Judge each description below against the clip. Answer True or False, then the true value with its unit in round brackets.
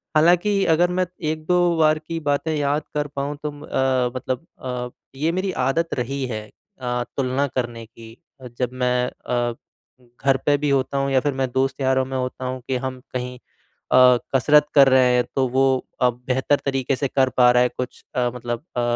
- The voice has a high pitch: False (130 Hz)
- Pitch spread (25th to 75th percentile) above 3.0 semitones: False (2.7 semitones)